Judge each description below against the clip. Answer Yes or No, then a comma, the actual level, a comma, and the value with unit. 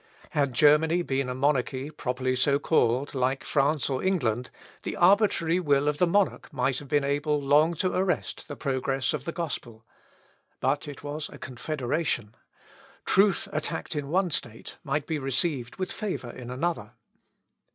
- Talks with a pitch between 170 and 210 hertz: No, medium, 145 Hz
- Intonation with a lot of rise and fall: No, average, 3.8 semitones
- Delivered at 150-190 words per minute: Yes, average, 160 wpm